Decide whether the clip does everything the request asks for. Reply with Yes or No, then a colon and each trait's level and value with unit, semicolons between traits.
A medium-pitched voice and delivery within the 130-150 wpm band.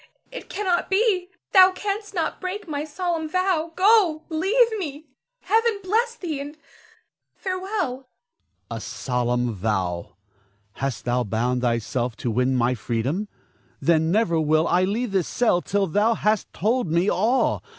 No: high, 245 Hz; average, 145 wpm